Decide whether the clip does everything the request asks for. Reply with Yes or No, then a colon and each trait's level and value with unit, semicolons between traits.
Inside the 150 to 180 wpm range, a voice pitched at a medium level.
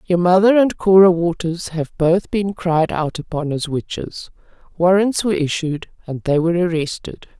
Yes: average, 160 wpm; medium, 175 Hz